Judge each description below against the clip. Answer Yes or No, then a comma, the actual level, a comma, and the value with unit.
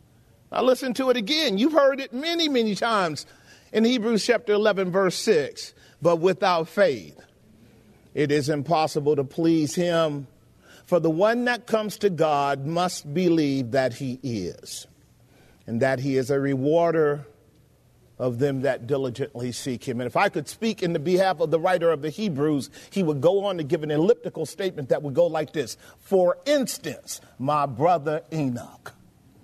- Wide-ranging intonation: Yes, wide, 6.4 semitones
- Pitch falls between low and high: Yes, medium, 160 Hz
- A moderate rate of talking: Yes, average, 170 wpm